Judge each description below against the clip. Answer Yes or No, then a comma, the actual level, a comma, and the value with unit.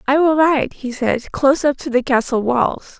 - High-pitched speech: Yes, very high, 270 Hz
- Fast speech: Yes, fast, 220 wpm